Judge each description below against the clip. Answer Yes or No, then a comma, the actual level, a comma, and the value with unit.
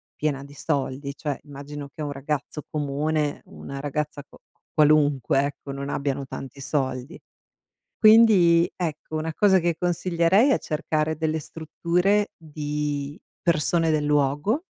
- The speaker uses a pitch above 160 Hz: No, medium, 150 Hz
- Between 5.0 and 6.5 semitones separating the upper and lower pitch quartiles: No, average, 2.8 semitones